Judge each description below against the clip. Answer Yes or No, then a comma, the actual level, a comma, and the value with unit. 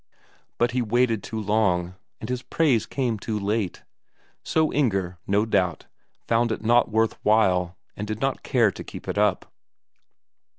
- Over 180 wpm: No, average, 160 wpm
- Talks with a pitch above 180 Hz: No, low, 110 Hz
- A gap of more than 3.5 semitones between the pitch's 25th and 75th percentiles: No, average, 3.2 semitones